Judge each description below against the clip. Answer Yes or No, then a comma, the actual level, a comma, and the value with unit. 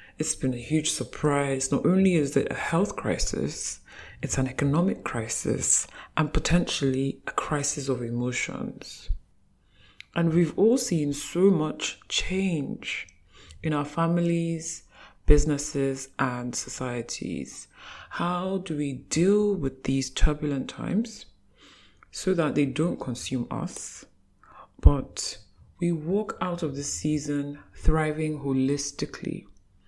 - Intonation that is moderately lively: Yes, average, 3.9 semitones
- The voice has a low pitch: No, medium, 145 Hz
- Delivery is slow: Yes, slow, 115 wpm